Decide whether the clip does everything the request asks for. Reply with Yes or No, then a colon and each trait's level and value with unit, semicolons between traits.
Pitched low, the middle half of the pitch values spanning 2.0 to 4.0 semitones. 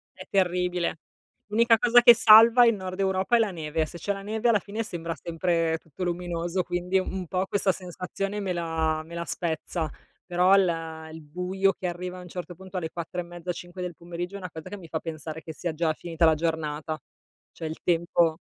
No: medium, 175 Hz; narrow, 2.6 semitones